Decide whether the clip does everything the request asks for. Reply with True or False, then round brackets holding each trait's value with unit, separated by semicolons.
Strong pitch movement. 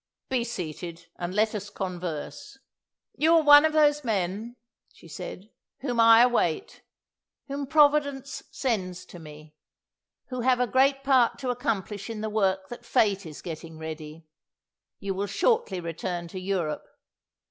True (6.8 semitones)